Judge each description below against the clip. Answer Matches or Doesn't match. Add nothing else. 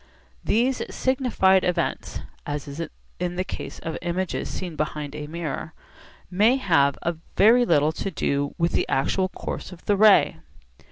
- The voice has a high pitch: Doesn't match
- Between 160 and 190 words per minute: Doesn't match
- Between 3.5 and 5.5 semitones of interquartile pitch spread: Matches